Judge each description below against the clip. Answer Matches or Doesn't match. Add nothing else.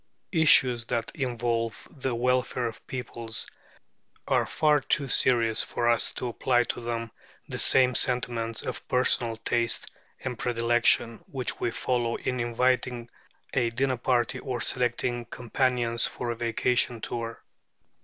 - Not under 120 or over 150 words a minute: Matches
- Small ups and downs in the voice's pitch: Matches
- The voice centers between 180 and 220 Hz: Doesn't match